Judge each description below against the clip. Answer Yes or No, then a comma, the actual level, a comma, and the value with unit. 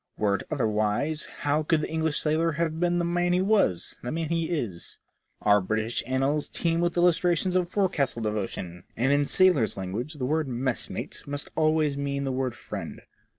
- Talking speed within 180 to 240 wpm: Yes, average, 185 wpm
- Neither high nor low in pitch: Yes, medium, 145 Hz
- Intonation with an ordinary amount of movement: No, wide, 5.7 semitones